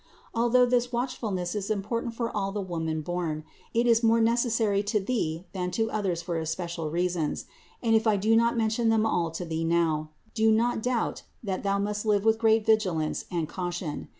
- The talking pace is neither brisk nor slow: Yes, average, 190 wpm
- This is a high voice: Yes, high, 205 Hz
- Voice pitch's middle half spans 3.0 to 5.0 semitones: Yes, average, 4.6 semitones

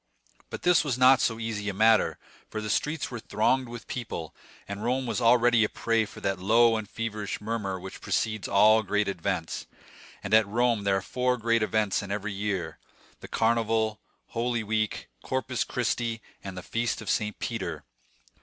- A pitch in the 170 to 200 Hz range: No, low, 110 Hz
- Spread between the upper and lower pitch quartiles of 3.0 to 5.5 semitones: No, narrow, 2.5 semitones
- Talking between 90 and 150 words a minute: No, average, 175 wpm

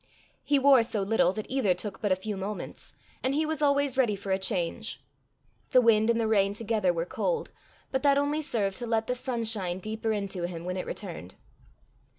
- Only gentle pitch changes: No, average, 4.9 semitones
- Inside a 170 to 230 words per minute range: Yes, average, 200 wpm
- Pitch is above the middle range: Yes, high, 220 Hz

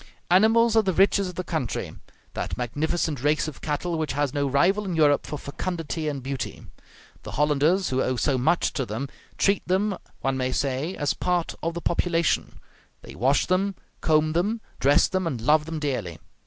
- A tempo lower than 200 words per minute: Yes, average, 185 wpm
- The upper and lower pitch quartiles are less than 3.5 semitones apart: No, average, 4.5 semitones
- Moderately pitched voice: Yes, medium, 155 Hz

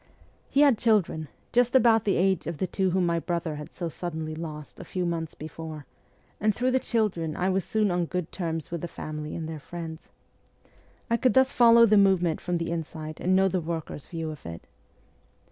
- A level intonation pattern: No, average, 3.9 semitones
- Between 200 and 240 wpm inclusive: Yes, fast, 205 wpm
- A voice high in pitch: No, medium, 175 Hz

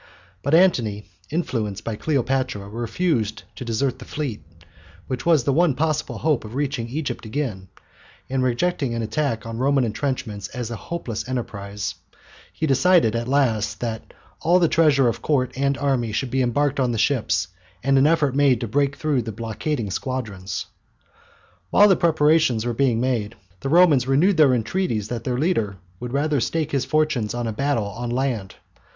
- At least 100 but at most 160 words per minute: No, average, 175 wpm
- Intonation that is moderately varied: Yes, average, 4.3 semitones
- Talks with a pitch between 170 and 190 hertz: No, low, 130 Hz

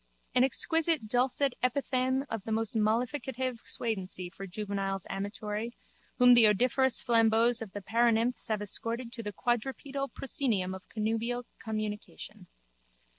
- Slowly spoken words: Yes, slow, 125 wpm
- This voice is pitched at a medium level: No, high, 230 Hz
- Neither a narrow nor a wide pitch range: Yes, average, 3.1 semitones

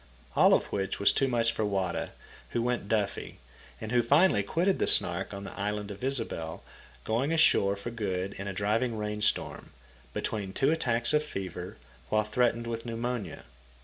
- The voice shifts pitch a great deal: No, average, 3.5 semitones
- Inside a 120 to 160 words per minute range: No, average, 175 wpm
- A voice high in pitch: No, low, 110 Hz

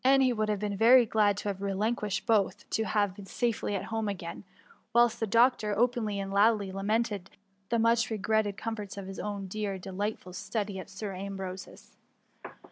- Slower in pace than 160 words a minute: No, average, 180 wpm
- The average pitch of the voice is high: Yes, high, 210 Hz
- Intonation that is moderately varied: No, narrow, 2.3 semitones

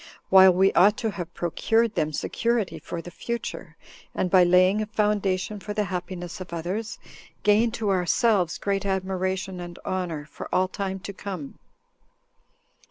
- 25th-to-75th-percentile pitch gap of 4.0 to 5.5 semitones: No, average, 2.7 semitones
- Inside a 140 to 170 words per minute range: Yes, average, 155 wpm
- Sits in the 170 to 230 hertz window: Yes, high, 190 Hz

